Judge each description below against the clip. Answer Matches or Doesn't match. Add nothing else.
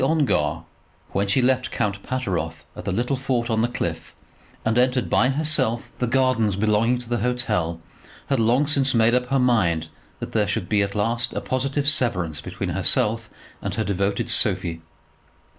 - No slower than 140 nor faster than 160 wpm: Doesn't match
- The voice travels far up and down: Doesn't match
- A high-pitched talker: Doesn't match